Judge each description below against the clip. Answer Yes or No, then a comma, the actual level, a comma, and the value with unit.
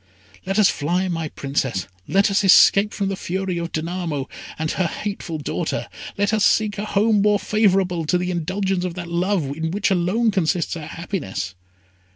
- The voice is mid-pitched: Yes, medium, 180 Hz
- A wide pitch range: No, average, 3.4 semitones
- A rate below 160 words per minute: No, average, 180 wpm